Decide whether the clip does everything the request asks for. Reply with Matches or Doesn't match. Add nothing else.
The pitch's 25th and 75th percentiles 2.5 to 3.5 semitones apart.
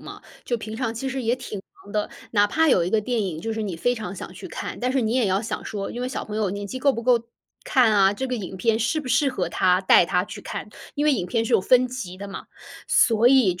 Doesn't match